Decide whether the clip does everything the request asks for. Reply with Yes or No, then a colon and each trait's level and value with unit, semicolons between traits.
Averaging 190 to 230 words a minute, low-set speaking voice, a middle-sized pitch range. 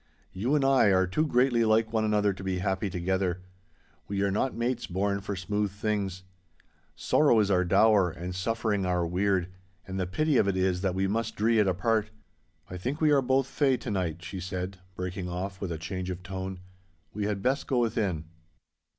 Yes: average, 200 wpm; low, 100 Hz; average, 3.4 semitones